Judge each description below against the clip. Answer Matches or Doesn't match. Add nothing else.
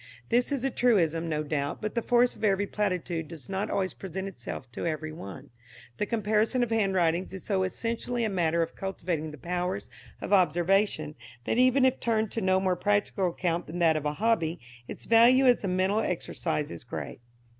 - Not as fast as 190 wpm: Doesn't match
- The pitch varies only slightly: Doesn't match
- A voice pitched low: Doesn't match